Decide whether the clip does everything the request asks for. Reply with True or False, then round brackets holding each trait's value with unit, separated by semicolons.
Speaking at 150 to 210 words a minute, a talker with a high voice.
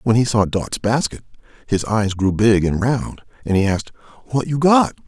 False (200 wpm; 115 Hz)